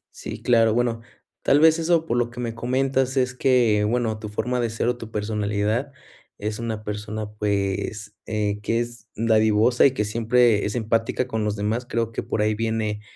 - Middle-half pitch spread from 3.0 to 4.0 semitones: No, narrow, 2.4 semitones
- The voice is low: Yes, low, 115 Hz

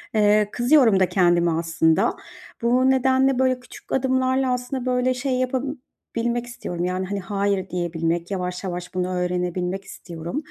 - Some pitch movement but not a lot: No, wide, 6.1 semitones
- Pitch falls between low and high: No, high, 205 Hz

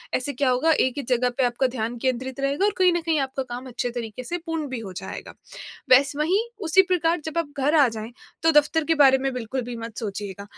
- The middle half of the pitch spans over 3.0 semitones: Yes, average, 4.5 semitones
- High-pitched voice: Yes, very high, 265 Hz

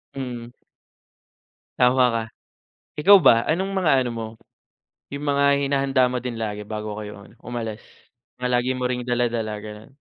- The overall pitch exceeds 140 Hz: No, low, 125 Hz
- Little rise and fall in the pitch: No, average, 3.3 semitones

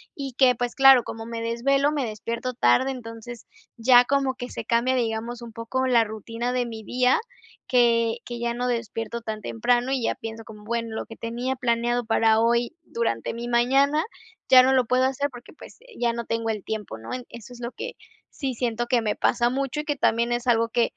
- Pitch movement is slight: Yes, narrow, 1.8 semitones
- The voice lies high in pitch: Yes, high, 235 Hz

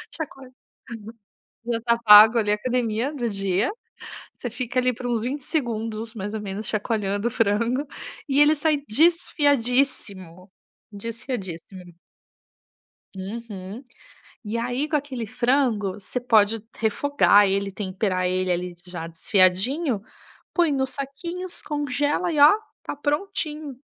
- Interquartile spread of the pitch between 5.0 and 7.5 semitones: Yes, wide, 5.4 semitones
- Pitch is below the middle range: No, high, 230 Hz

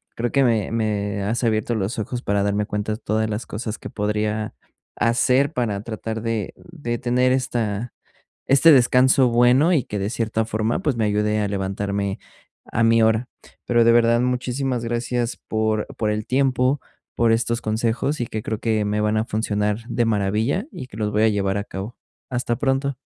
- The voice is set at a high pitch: No, low, 115 Hz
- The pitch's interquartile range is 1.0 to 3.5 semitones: Yes, narrow, 2.5 semitones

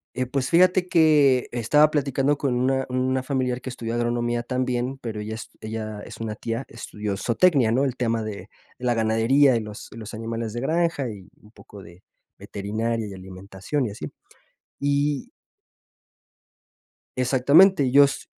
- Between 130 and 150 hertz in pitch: No, low, 120 Hz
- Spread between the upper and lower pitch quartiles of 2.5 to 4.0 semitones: Yes, average, 3.7 semitones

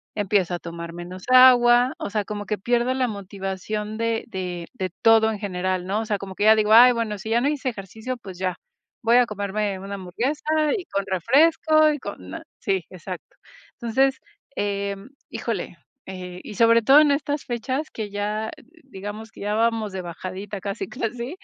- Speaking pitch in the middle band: No, high, 210 Hz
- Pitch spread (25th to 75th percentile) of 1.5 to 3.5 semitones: No, average, 3.9 semitones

